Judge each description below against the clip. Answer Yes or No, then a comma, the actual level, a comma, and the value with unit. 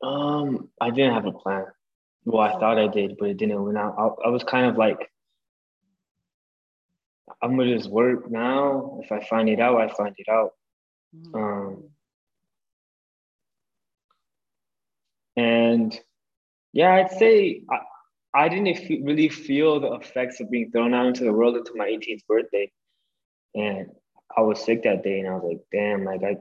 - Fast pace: No, average, 165 wpm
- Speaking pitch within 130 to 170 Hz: No, low, 115 Hz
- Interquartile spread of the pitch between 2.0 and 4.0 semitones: No, average, 5.2 semitones